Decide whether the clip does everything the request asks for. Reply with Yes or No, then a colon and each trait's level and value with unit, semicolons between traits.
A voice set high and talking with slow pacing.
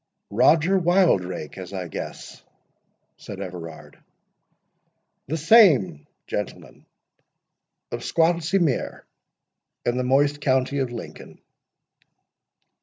No: low, 135 Hz; slow, 85 wpm